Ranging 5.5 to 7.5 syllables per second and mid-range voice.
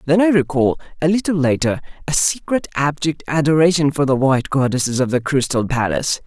Yes: 5.8 syllables/s; medium, 145 Hz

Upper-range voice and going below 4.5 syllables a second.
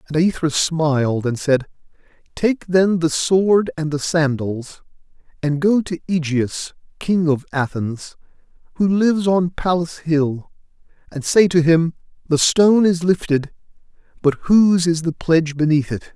No: medium, 165 Hz; 4.3 syllables/s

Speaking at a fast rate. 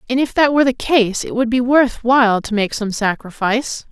Yes: fast, 230 wpm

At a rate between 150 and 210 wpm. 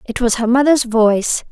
Yes: average, 200 wpm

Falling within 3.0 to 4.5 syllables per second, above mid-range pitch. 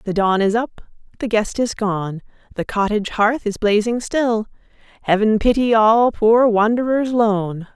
Yes: 4.2 syllables/s; high, 220 Hz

